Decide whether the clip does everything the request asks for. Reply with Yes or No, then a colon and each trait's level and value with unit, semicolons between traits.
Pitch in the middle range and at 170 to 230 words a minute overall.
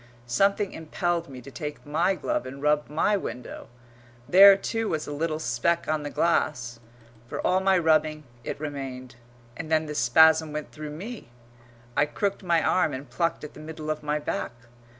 Yes: medium, 155 Hz; average, 180 wpm